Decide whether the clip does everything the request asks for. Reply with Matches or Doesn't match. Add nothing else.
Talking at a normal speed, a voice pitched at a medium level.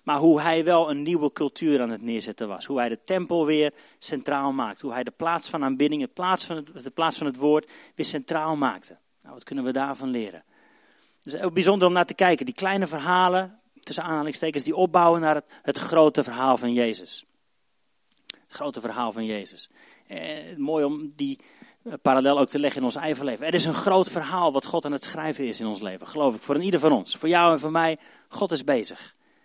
Doesn't match